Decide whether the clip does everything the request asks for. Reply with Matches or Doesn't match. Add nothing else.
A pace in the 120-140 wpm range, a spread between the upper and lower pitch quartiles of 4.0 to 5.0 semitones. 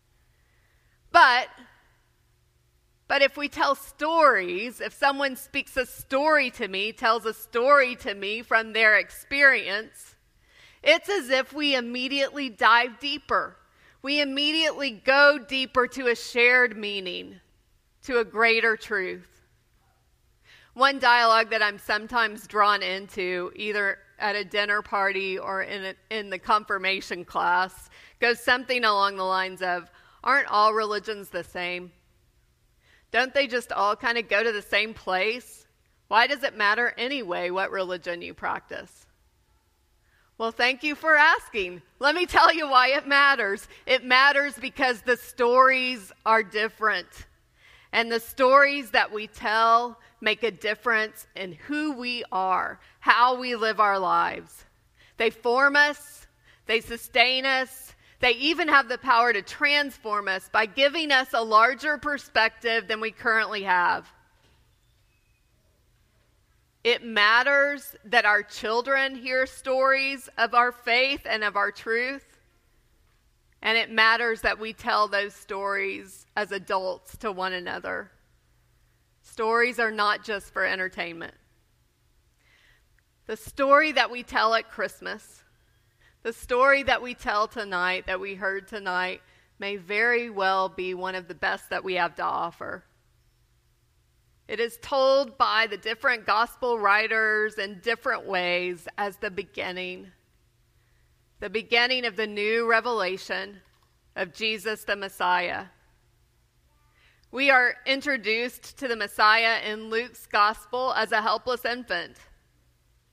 Matches